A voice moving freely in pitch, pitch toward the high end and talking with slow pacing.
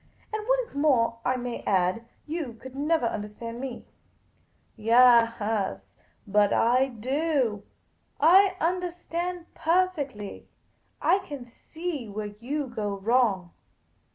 Yes: wide, 6.5 semitones; very high, 250 Hz; slow, 120 wpm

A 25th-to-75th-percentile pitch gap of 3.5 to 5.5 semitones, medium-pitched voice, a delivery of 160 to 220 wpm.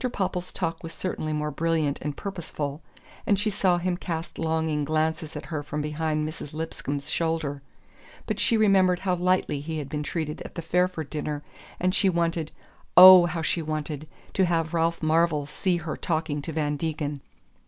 No: narrow, 2.6 semitones; medium, 160 Hz; average, 175 wpm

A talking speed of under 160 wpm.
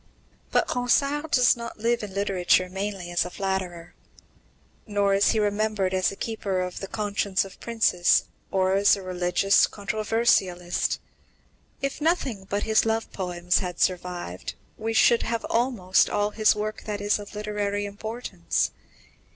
Yes: average, 150 wpm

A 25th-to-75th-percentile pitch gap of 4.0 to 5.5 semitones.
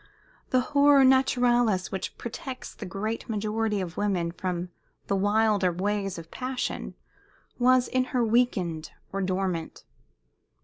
Yes: average, 4.9 semitones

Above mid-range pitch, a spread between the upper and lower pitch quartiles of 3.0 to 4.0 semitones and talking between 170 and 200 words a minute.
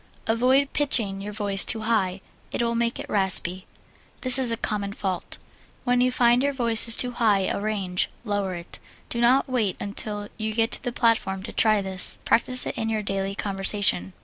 Yes: high, 215 Hz; average, 3.4 semitones; average, 195 wpm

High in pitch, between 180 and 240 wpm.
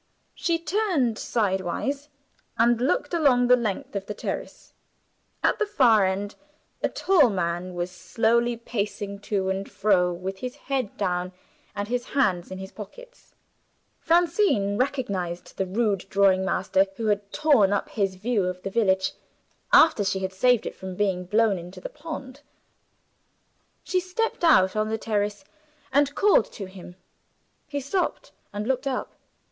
No: high, 210 Hz; average, 150 wpm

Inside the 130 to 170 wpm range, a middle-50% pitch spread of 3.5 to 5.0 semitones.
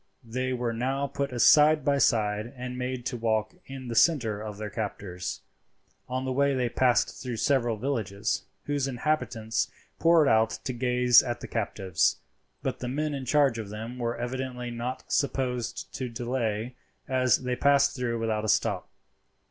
No: average, 165 wpm; average, 2.8 semitones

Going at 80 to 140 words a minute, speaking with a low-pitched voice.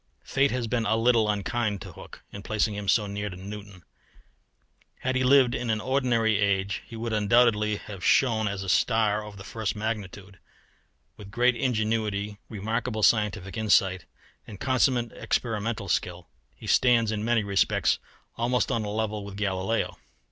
No: average, 160 wpm; low, 110 Hz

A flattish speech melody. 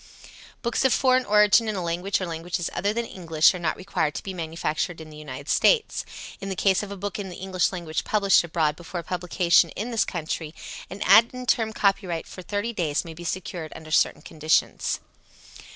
No: average, 3.8 semitones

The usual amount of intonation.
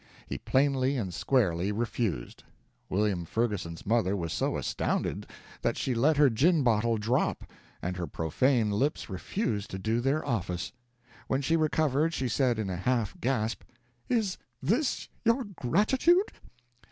No: wide, 6.1 semitones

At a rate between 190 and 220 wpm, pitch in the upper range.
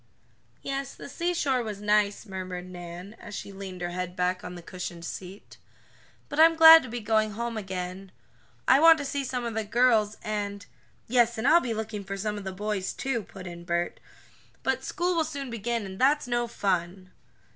Yes: average, 200 wpm; high, 210 Hz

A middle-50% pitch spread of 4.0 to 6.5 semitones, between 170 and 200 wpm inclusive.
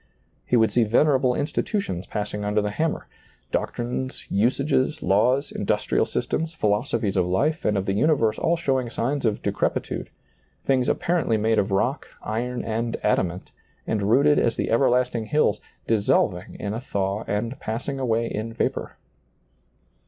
No: average, 4.3 semitones; average, 150 wpm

